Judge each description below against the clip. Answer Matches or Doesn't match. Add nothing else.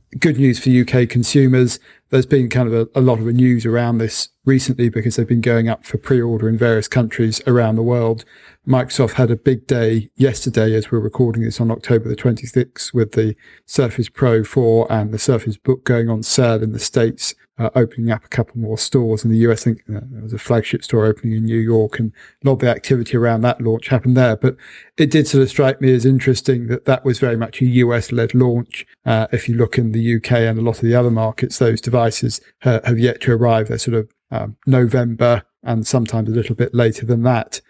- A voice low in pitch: Matches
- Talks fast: Matches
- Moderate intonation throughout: Doesn't match